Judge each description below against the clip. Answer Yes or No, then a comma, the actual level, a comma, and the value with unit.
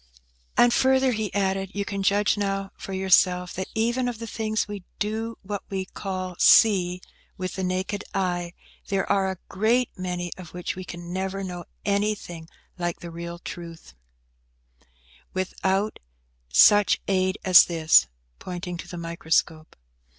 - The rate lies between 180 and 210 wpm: No, average, 150 wpm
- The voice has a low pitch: No, high, 190 Hz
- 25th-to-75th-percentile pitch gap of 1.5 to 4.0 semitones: Yes, narrow, 2.5 semitones